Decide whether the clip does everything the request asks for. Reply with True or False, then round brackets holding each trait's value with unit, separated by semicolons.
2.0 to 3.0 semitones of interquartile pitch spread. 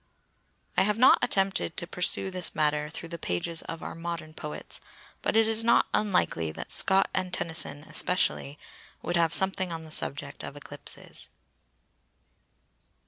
False (3.5 semitones)